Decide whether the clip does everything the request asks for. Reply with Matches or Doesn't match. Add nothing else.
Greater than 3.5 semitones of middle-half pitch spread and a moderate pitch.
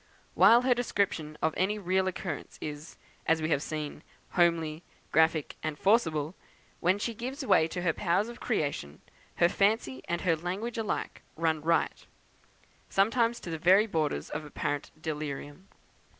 Matches